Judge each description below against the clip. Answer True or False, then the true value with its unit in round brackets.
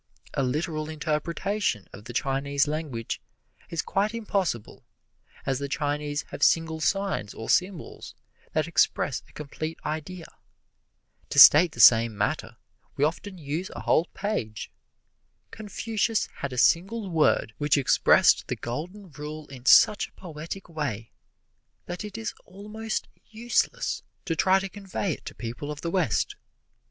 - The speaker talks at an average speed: True (145 wpm)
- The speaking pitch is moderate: True (155 Hz)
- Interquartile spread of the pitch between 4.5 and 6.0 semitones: True (5.4 semitones)